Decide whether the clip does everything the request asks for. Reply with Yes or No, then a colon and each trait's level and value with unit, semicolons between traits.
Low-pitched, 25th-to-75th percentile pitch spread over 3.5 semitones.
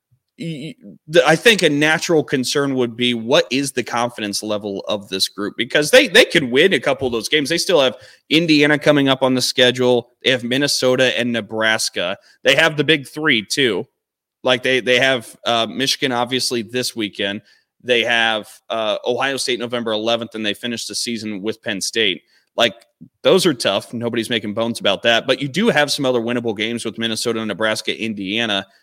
No: low, 120 Hz; average, 3.2 semitones